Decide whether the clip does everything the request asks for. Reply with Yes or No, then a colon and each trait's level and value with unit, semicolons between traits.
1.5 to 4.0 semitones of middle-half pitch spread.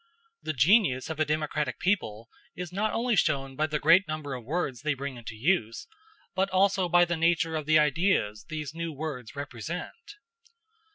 No: average, 4.6 semitones